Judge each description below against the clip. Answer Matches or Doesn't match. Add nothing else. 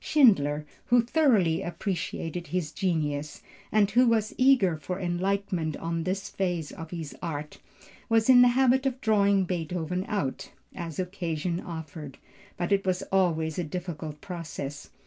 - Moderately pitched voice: Matches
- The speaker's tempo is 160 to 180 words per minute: Doesn't match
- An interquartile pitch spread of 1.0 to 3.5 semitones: Doesn't match